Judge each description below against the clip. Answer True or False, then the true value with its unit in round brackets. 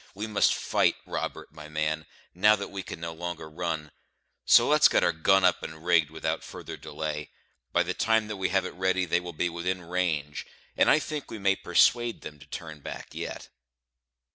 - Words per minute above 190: True (200 wpm)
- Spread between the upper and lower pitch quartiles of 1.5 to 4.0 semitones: True (3.3 semitones)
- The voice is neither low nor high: False (85 Hz)